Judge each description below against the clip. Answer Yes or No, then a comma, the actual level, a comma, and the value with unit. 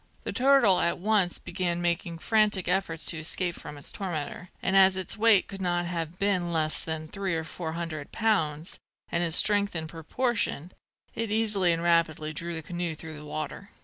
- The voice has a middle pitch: Yes, medium, 175 Hz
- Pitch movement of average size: Yes, average, 3.5 semitones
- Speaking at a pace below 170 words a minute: No, average, 185 wpm